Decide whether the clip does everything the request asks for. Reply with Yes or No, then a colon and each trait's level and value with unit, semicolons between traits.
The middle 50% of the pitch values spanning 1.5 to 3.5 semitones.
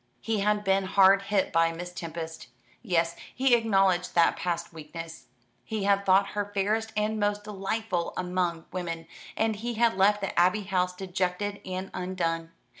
Yes: average, 2.9 semitones